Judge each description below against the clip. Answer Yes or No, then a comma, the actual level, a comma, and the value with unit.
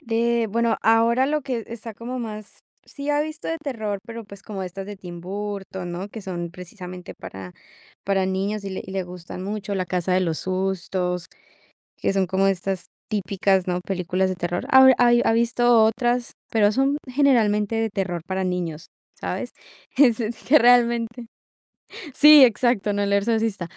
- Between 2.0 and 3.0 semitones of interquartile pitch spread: No, average, 4.0 semitones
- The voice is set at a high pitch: Yes, high, 205 Hz